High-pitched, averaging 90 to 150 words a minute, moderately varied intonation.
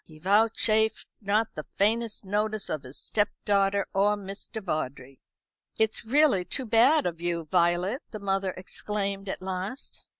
Yes: high, 200 Hz; average, 140 wpm; average, 3.2 semitones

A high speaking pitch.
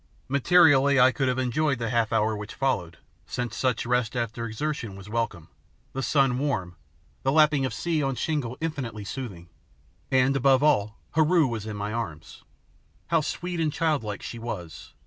No: low, 125 Hz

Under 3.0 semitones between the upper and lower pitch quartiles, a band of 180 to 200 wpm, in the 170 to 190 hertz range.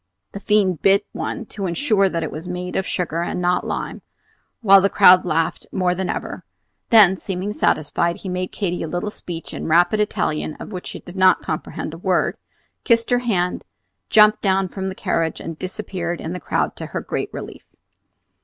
Yes: narrow, 2.4 semitones; average, 190 wpm; medium, 185 Hz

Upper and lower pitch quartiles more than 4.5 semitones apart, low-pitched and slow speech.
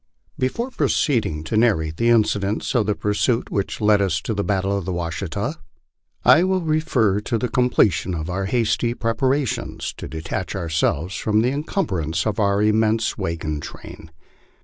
No: average, 5.3 semitones; low, 105 Hz; average, 165 wpm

